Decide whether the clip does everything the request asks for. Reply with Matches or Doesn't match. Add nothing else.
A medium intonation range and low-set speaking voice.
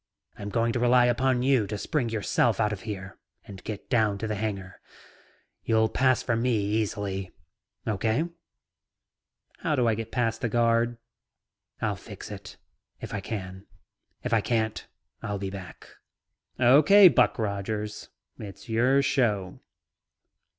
Matches